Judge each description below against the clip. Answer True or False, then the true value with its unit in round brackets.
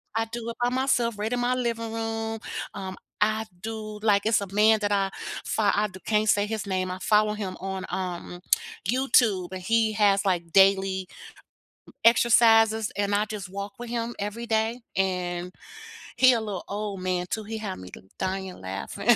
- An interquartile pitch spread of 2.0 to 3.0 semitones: True (2.7 semitones)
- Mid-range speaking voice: False (210 Hz)